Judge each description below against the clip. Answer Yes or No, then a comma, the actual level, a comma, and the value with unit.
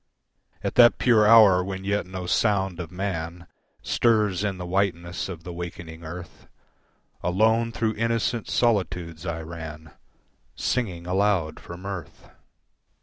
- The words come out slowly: Yes, slow, 130 wpm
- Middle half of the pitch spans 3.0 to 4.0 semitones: Yes, average, 3.5 semitones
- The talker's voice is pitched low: Yes, very low, 95 Hz